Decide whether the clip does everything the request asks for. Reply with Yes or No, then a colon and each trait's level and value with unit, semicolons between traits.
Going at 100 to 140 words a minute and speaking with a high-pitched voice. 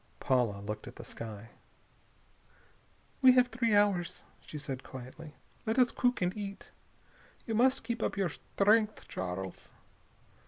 Yes: slow, 135 wpm; high, 195 Hz